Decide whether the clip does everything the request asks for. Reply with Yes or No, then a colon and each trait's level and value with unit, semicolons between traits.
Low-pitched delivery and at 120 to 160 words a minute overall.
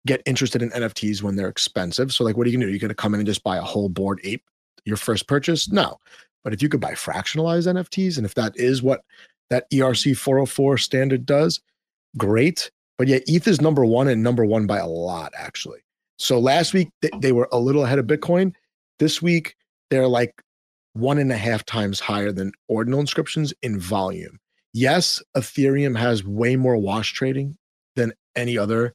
No: low, 125 Hz; fast, 205 wpm